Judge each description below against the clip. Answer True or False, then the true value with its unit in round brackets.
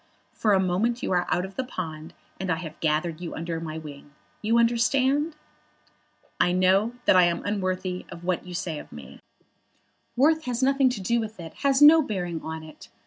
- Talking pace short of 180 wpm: False (195 wpm)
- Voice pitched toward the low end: False (185 Hz)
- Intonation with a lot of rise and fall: True (5.9 semitones)